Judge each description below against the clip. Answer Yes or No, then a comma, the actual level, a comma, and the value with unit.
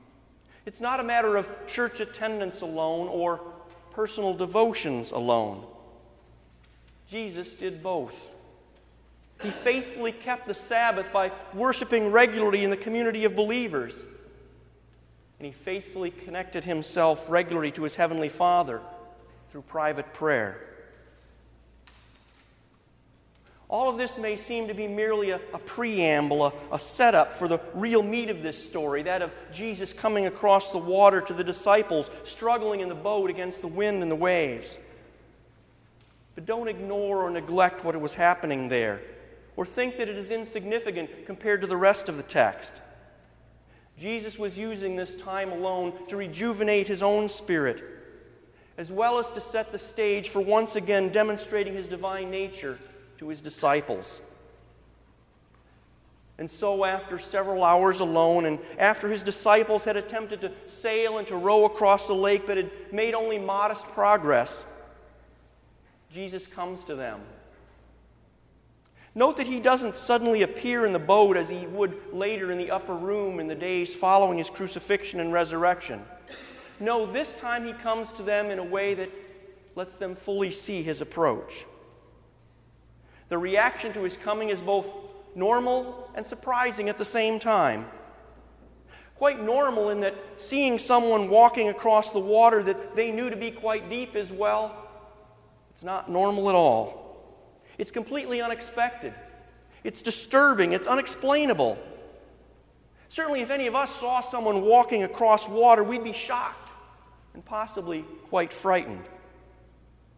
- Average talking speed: Yes, average, 145 wpm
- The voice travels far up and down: No, average, 4.0 semitones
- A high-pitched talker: Yes, high, 200 Hz